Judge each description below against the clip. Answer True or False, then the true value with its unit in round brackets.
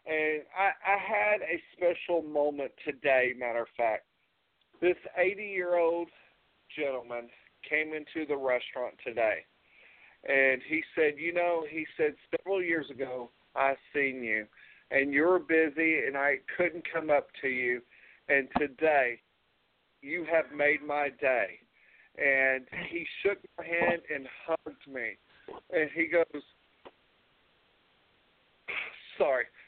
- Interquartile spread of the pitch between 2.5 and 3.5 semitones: False (4.1 semitones)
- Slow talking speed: True (125 wpm)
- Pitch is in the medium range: True (155 Hz)